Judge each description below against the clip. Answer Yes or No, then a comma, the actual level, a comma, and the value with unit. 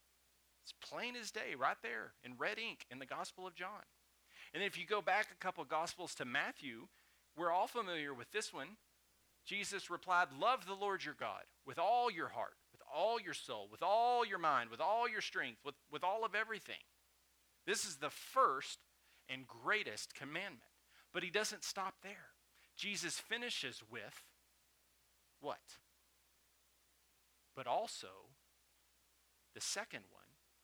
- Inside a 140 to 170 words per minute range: Yes, average, 155 wpm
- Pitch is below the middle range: No, medium, 155 Hz